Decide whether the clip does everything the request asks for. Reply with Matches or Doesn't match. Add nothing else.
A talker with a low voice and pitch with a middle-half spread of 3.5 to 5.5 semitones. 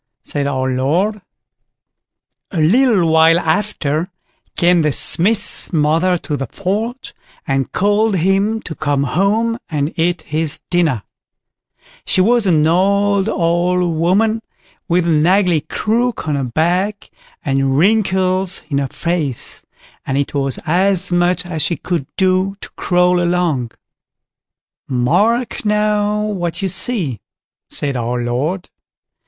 Doesn't match